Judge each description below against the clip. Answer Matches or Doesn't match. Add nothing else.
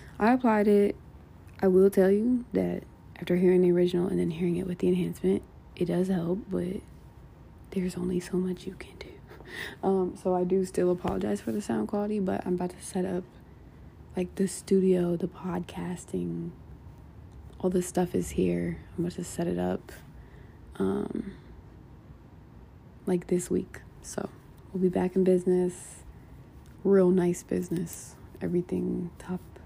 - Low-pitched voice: Doesn't match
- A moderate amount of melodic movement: Doesn't match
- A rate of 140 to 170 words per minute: Matches